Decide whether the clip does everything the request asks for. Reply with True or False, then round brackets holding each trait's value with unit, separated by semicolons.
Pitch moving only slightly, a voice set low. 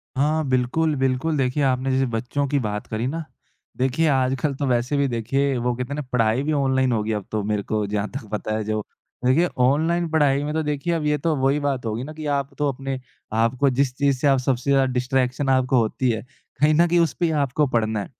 False (3.0 semitones; 130 Hz)